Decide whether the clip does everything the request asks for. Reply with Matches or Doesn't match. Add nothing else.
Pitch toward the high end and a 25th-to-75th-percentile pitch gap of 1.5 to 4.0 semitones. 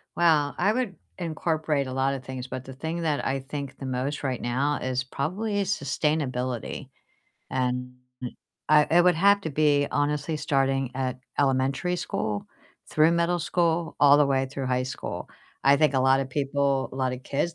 Doesn't match